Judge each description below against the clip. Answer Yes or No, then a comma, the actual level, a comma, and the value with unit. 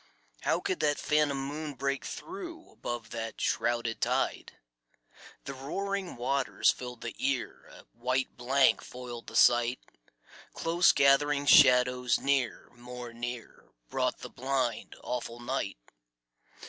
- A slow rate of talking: Yes, slow, 120 wpm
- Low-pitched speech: Yes, low, 130 Hz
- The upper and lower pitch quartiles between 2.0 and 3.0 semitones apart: Yes, average, 2.7 semitones